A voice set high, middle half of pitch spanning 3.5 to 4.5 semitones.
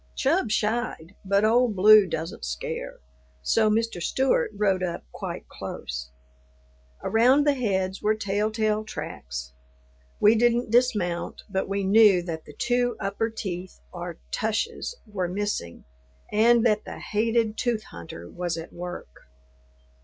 Yes: high, 210 Hz; average, 4.2 semitones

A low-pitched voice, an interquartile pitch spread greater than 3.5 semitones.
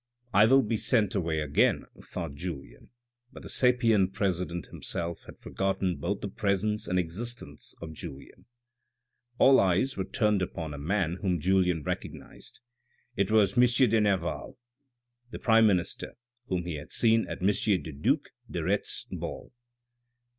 Yes: very low, 95 Hz; average, 4.2 semitones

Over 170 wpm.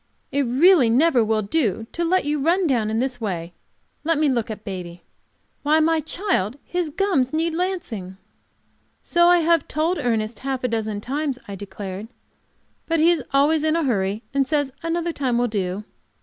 Yes: average, 180 wpm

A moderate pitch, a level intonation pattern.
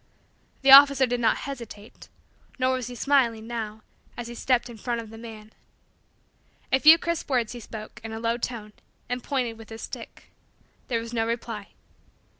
No: high, 235 Hz; narrow, 2.3 semitones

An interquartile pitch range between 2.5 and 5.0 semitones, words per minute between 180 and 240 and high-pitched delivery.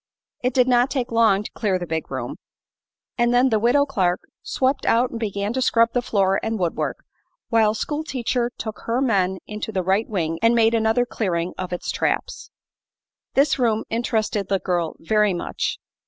Yes: average, 3.9 semitones; average, 185 wpm; high, 220 Hz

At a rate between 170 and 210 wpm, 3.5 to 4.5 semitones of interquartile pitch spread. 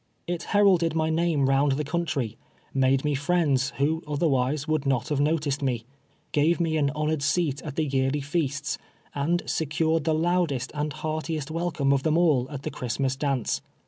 No: average, 190 wpm; average, 2.7 semitones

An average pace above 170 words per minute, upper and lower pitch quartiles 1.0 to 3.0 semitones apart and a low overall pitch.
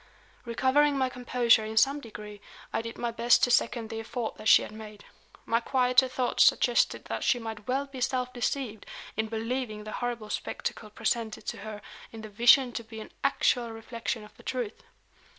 No: average, 185 wpm; narrow, 2.4 semitones; high, 235 Hz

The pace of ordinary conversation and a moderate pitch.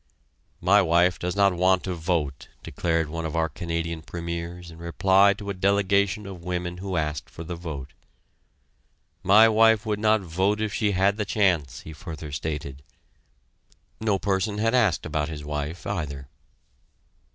No: average, 160 wpm; very low, 90 Hz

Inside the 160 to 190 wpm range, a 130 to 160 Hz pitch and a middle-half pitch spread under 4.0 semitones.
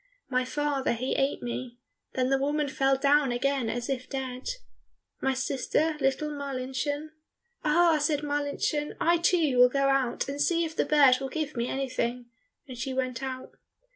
No: average, 170 wpm; very high, 270 Hz; narrow, 2.5 semitones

